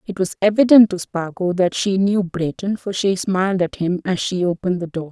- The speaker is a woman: Yes, female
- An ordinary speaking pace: No, fast, 225 wpm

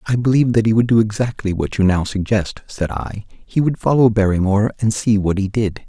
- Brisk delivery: Yes, fast, 225 wpm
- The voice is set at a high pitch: No, low, 105 Hz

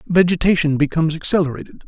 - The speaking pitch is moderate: Yes, medium, 160 Hz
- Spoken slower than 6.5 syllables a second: No, 7.0 syllables/s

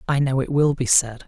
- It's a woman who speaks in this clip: No, male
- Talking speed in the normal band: No, fast, 280 wpm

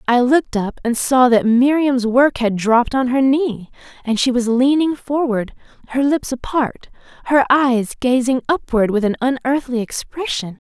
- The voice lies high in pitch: Yes, very high, 255 Hz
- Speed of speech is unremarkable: Yes, average, 165 wpm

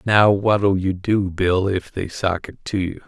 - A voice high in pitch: No, very low, 95 Hz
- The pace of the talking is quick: Yes, fast, 215 wpm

